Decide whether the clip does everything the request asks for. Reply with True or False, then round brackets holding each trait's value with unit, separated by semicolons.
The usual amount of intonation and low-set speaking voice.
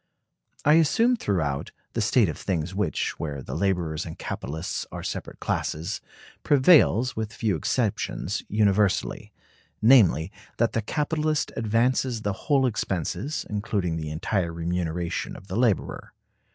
False (6.2 semitones; 100 Hz)